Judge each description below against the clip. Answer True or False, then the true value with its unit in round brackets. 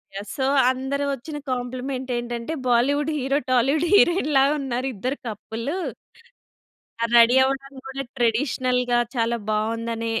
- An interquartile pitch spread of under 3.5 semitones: True (2.7 semitones)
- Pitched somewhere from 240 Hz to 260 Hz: True (255 Hz)